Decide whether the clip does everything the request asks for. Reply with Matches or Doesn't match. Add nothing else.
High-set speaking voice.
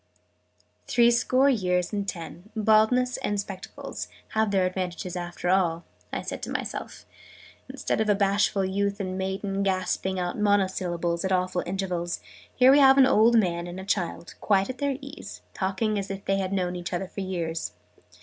Matches